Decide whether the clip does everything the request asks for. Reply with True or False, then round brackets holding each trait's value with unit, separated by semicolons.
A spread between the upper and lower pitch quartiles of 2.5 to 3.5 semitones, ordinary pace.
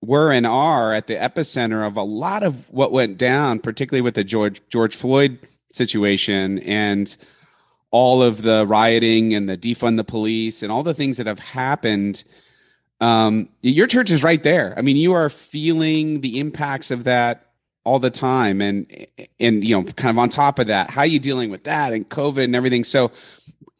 False (3.9 semitones; 190 wpm)